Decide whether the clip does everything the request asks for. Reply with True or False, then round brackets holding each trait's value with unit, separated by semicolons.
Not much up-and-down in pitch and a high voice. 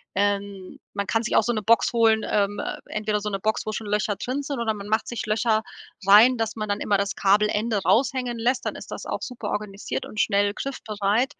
True (2.2 semitones; 215 Hz)